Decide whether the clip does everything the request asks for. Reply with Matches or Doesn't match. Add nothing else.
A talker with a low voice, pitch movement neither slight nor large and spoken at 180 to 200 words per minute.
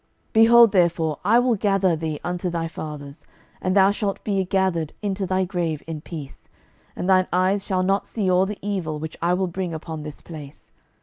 Doesn't match